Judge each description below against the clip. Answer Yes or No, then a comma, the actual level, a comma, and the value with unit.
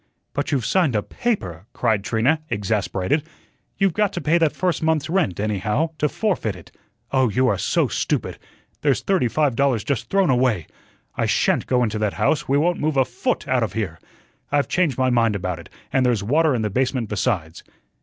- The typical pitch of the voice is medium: No, low, 125 Hz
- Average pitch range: No, wide, 6.5 semitones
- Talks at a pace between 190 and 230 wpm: Yes, average, 195 wpm